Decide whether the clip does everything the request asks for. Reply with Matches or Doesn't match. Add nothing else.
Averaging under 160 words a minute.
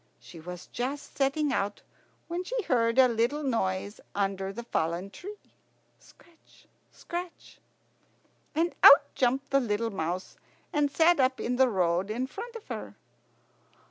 Matches